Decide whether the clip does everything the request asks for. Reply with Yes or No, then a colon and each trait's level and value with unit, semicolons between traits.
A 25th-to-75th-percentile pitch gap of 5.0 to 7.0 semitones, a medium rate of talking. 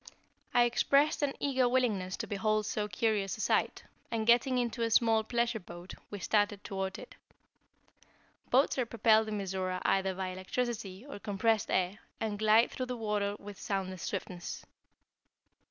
No: average, 3.5 semitones; average, 155 wpm